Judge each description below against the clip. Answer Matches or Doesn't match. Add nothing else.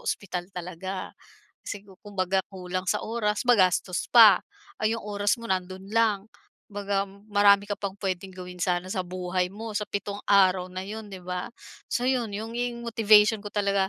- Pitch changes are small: Matches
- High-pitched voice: Matches